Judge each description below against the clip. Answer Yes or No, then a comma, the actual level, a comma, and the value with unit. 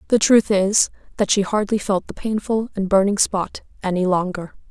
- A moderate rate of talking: Yes, average, 180 wpm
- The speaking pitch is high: Yes, high, 200 Hz